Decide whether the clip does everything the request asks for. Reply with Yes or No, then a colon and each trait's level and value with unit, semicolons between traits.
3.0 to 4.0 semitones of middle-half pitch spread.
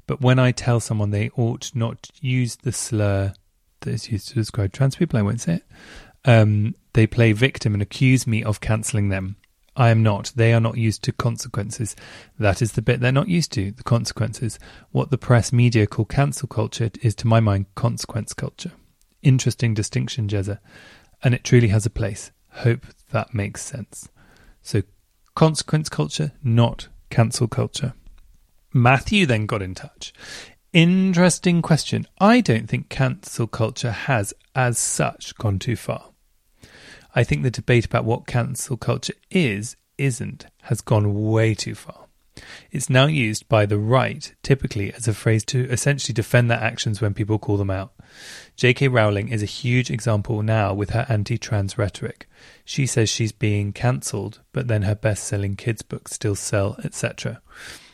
Yes: average, 3.4 semitones